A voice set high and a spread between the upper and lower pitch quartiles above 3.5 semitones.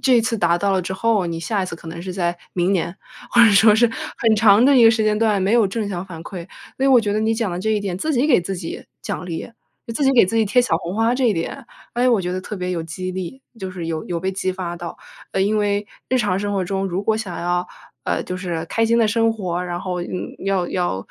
Yes: high, 195 Hz; average, 4.0 semitones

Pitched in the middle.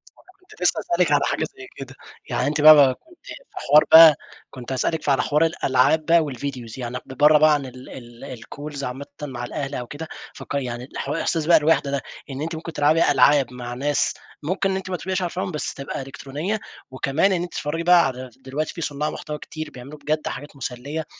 Yes: medium, 145 Hz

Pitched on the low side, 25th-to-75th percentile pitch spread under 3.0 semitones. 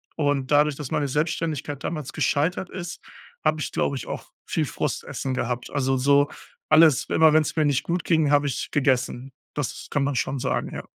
No: medium, 145 Hz; narrow, 2.4 semitones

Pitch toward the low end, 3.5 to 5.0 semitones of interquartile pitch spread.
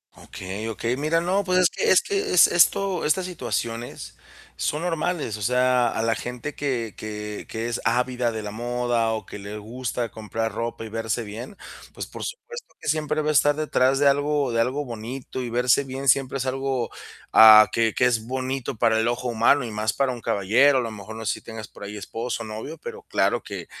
Yes: low, 120 Hz; average, 4.0 semitones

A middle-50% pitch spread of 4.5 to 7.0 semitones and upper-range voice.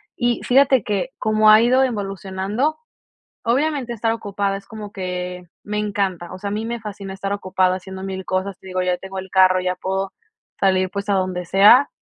No: narrow, 2.5 semitones; high, 195 Hz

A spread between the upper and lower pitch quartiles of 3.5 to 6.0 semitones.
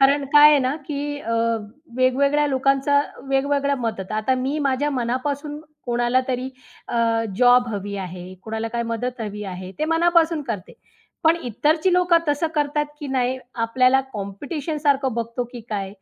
Yes: average, 4.1 semitones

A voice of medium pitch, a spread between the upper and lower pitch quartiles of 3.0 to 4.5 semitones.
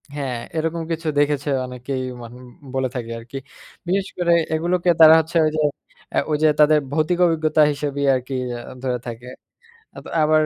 Yes: medium, 150 Hz; average, 3.6 semitones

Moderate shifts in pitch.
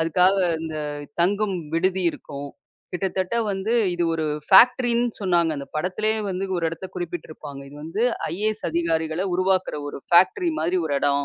Yes: average, 3.3 semitones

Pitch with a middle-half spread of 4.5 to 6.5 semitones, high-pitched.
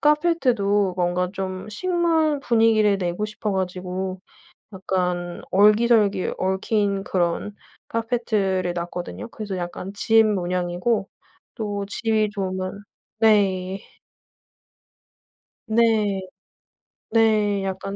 No: average, 2.9 semitones; high, 200 Hz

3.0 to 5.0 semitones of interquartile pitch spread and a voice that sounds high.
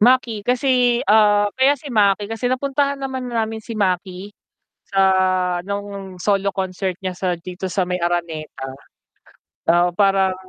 Yes: average, 4.6 semitones; high, 200 Hz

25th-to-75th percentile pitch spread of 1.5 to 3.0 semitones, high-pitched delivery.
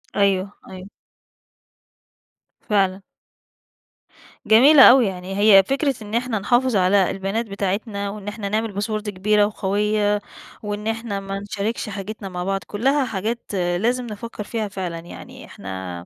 Yes: narrow, 2.4 semitones; high, 205 Hz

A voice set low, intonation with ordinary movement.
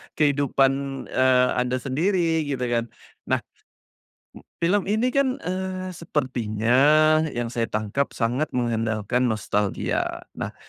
No: low, 130 Hz; wide, 5.8 semitones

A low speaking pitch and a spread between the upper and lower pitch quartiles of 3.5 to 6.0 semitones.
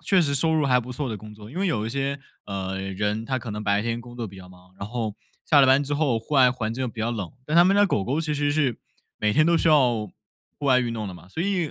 Yes: low, 125 Hz; wide, 5.4 semitones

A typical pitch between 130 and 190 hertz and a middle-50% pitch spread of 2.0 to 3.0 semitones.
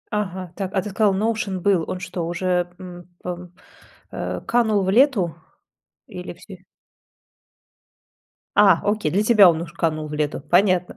Yes: medium, 185 Hz; average, 2.7 semitones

